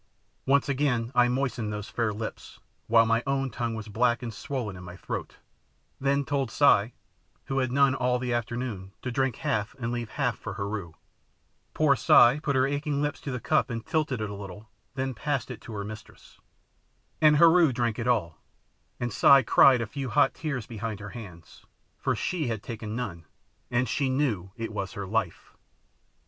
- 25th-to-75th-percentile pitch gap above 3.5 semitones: Yes, average, 4.0 semitones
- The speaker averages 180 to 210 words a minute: Yes, average, 190 wpm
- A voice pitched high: No, low, 120 Hz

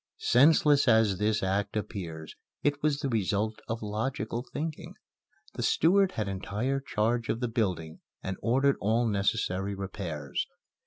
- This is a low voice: Yes, low, 110 Hz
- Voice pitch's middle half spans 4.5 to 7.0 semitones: Yes, average, 5.0 semitones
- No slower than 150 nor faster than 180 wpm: No, average, 140 wpm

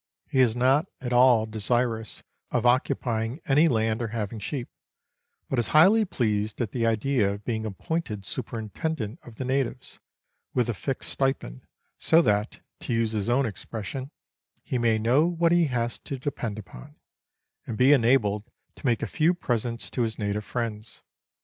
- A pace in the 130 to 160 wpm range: No, average, 170 wpm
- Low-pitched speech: Yes, low, 120 Hz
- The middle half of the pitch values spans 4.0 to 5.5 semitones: No, average, 3.4 semitones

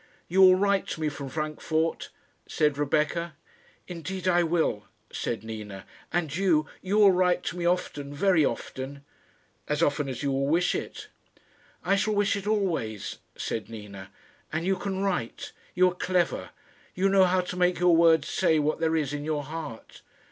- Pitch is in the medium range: Yes, medium, 165 Hz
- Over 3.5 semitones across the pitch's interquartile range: Yes, average, 4.2 semitones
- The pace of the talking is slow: No, average, 175 wpm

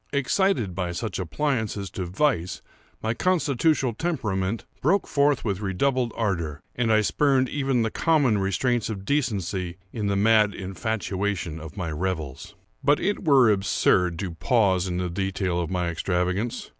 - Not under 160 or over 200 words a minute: No, average, 150 wpm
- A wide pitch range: Yes, wide, 5.9 semitones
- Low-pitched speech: Yes, low, 105 Hz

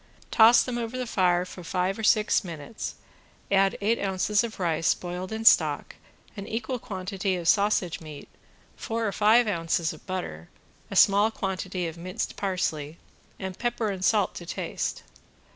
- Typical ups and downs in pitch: Yes, average, 3.7 semitones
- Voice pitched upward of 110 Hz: Yes, high, 190 Hz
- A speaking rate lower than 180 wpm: Yes, average, 160 wpm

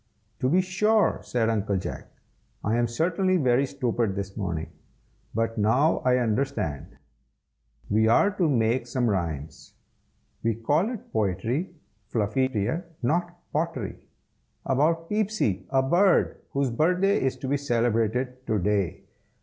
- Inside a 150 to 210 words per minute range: No, slow, 135 wpm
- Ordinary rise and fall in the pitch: No, wide, 7.1 semitones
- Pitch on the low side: Yes, low, 125 Hz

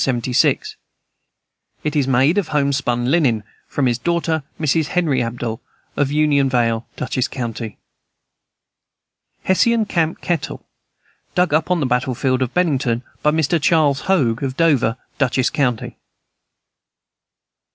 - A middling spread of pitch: Yes, average, 4.6 semitones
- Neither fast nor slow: No, slow, 120 wpm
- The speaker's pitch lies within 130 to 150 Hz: Yes, medium, 140 Hz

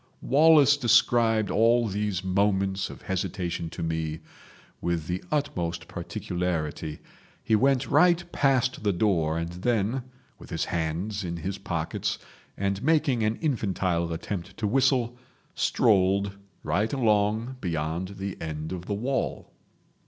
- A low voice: Yes, low, 100 Hz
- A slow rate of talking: Yes, slow, 130 wpm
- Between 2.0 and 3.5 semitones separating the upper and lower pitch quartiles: No, wide, 5.6 semitones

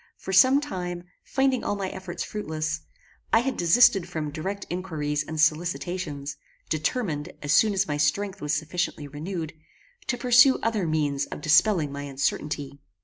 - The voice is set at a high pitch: No, medium, 165 Hz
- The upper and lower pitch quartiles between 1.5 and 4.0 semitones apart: No, average, 5.0 semitones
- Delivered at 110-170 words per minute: Yes, average, 150 wpm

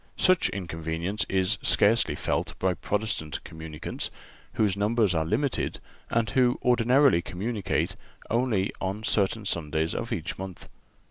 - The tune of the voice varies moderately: Yes, average, 4.6 semitones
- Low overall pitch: Yes, low, 100 Hz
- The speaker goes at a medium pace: No, slow, 125 wpm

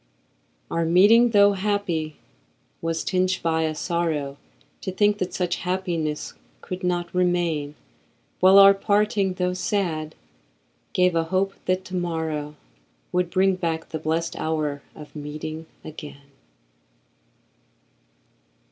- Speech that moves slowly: Yes, slow, 120 wpm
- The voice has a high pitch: No, medium, 175 Hz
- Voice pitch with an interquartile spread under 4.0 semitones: Yes, average, 2.9 semitones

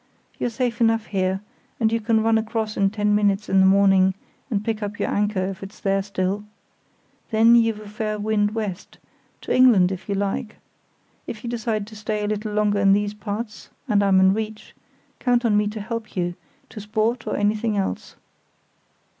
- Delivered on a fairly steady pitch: Yes, narrow, 1.9 semitones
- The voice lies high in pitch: Yes, high, 210 Hz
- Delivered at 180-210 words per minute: Yes, average, 190 wpm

